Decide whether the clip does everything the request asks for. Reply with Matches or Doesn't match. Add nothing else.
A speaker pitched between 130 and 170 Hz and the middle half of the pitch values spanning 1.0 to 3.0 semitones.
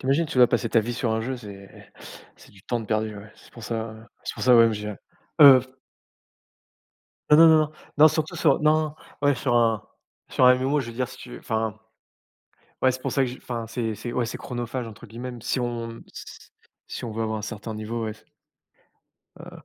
Doesn't match